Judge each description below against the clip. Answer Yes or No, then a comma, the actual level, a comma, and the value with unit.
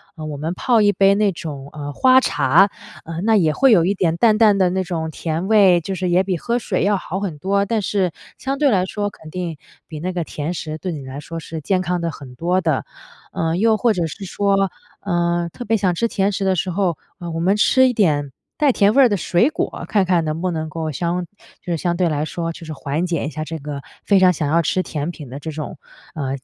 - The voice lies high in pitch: No, medium, 175 Hz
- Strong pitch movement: No, average, 4.0 semitones